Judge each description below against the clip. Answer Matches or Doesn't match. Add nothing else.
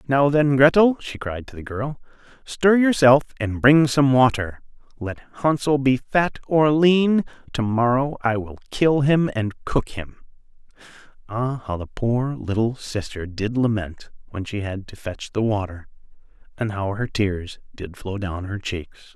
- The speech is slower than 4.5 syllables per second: Matches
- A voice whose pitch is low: Matches